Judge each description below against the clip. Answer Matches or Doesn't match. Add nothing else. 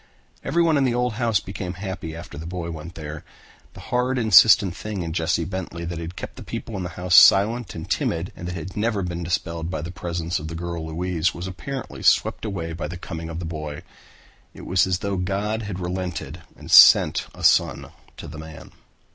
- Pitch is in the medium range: Doesn't match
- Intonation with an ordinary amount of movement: Matches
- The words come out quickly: Matches